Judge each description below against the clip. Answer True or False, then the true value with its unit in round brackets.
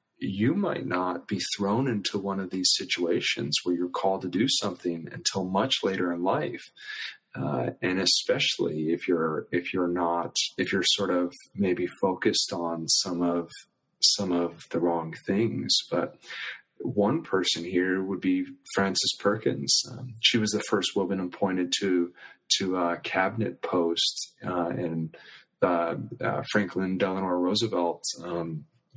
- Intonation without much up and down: True (2.0 semitones)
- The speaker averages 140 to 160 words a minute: True (150 wpm)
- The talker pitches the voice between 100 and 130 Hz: False (90 Hz)